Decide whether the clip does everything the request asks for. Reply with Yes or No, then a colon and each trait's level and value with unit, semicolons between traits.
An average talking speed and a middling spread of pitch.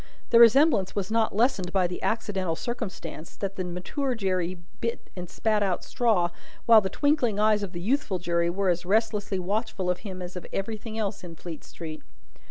Yes: average, 185 wpm; average, 3.7 semitones